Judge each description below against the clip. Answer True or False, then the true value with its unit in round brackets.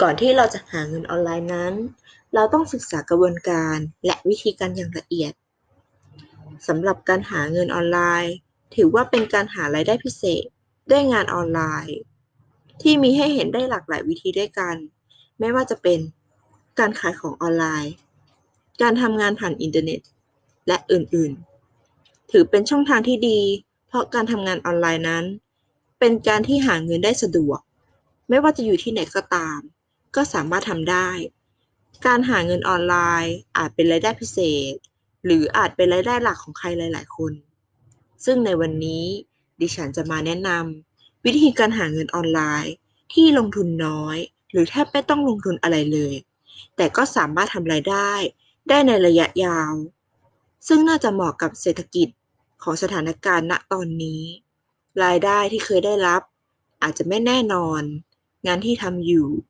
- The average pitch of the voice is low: False (175 Hz)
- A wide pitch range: True (5.7 semitones)